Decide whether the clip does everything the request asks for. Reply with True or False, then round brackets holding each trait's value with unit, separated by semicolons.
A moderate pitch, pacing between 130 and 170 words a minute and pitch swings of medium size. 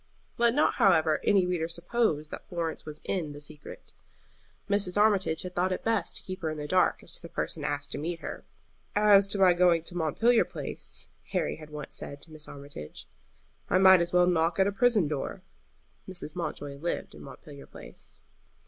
False (175 Hz; 195 wpm; 3.7 semitones)